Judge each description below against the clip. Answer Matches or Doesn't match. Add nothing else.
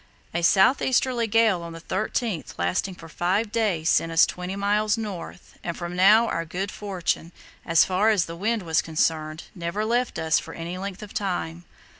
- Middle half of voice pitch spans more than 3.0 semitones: Matches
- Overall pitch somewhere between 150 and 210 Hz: Matches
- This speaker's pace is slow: Doesn't match